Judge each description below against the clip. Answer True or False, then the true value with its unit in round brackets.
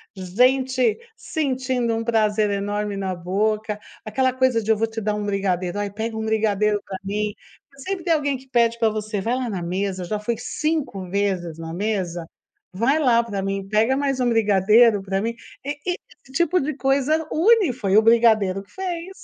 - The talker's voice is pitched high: True (220 Hz)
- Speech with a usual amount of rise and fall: True (4.5 semitones)